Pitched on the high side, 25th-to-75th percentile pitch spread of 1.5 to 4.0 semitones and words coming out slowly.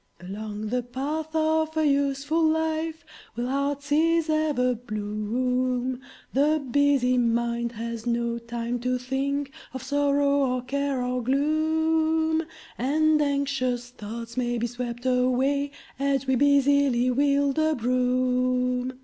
Yes: very high, 260 Hz; average, 2.8 semitones; slow, 125 wpm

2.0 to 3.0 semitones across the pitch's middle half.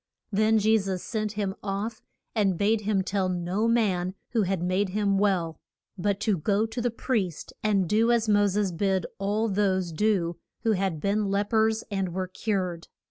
Yes: narrow, 2.5 semitones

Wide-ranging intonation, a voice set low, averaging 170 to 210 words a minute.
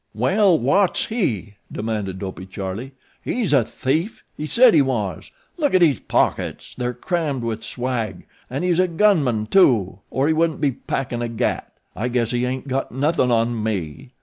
Yes: wide, 6.3 semitones; low, 130 Hz; average, 175 wpm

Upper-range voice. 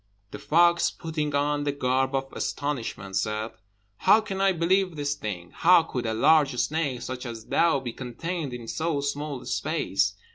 No: medium, 145 Hz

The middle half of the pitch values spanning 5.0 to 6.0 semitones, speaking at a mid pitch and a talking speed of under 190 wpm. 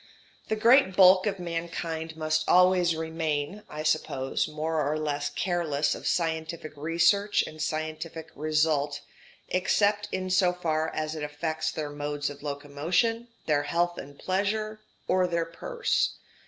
No: average, 3.1 semitones; medium, 160 Hz; average, 140 wpm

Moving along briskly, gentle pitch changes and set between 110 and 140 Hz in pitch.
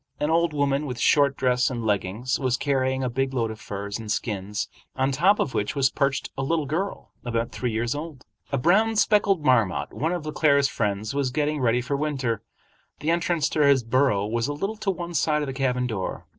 No: fast, 215 wpm; average, 4.3 semitones; low, 135 Hz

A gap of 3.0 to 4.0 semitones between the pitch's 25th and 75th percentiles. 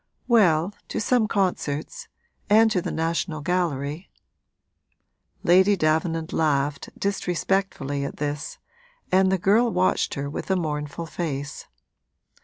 No: average, 4.6 semitones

